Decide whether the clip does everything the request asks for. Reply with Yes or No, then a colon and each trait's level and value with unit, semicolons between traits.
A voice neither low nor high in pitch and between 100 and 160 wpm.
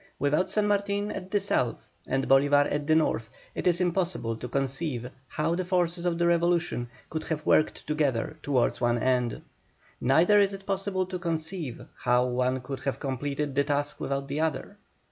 No: medium, 150 Hz; average, 180 wpm